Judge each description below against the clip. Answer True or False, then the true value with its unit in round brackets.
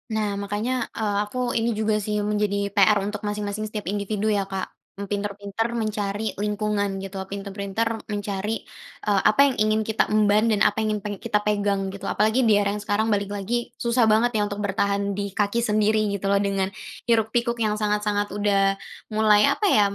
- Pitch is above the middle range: True (210 Hz)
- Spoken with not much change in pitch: True (1.2 semitones)